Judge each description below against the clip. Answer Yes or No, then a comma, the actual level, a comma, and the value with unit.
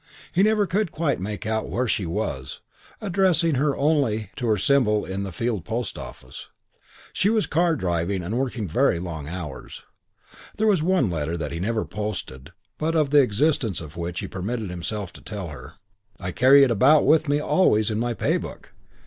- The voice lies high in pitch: No, low, 110 Hz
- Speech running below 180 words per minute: No, average, 190 wpm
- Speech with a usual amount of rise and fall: No, wide, 8.4 semitones